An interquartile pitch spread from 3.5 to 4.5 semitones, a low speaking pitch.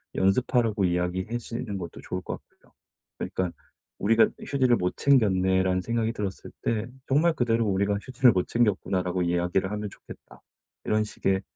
Yes: average, 3.9 semitones; low, 100 Hz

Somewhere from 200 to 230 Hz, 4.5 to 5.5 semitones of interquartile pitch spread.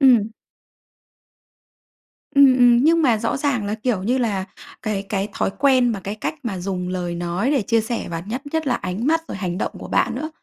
Yes: high, 225 Hz; average, 5.2 semitones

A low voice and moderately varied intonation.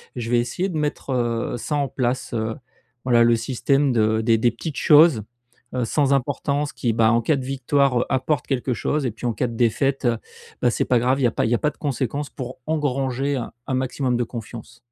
Yes: low, 125 Hz; average, 3.0 semitones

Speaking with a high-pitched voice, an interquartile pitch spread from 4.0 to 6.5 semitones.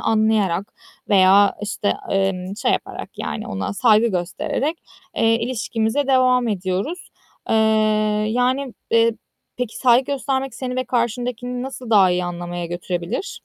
Yes: high, 220 Hz; average, 4.4 semitones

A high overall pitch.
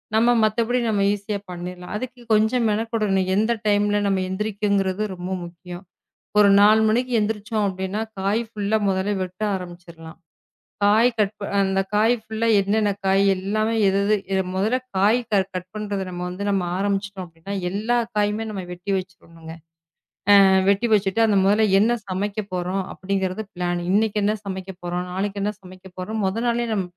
Yes: high, 200 Hz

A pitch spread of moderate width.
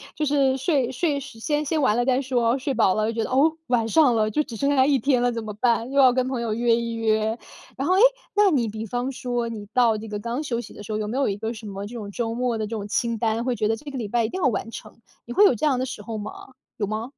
Yes: average, 3.2 semitones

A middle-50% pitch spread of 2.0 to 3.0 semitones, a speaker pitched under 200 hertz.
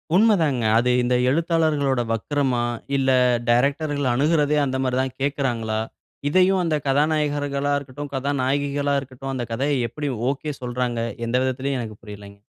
Yes: narrow, 2.6 semitones; medium, 140 Hz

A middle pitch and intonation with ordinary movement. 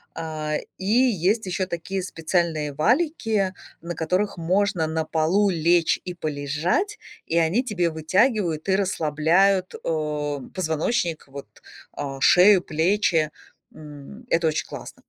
Yes: medium, 170 Hz; average, 3.8 semitones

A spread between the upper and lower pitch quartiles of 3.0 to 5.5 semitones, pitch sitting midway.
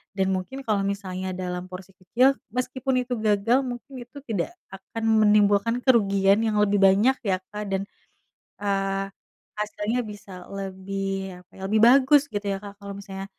No: average, 3.3 semitones; high, 200 Hz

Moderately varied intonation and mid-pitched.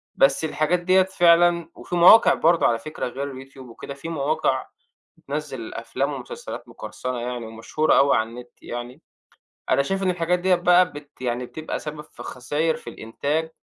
Yes: average, 5.0 semitones; medium, 150 Hz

